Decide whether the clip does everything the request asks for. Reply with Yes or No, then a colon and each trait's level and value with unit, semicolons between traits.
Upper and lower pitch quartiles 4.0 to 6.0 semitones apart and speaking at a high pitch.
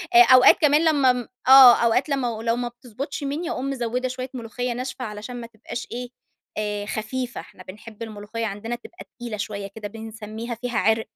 No: average, 2.7 semitones; high, 240 Hz